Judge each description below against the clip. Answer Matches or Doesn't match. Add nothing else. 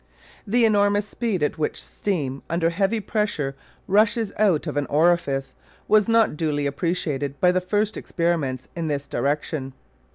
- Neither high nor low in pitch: Matches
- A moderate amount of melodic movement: Doesn't match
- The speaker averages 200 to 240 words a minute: Doesn't match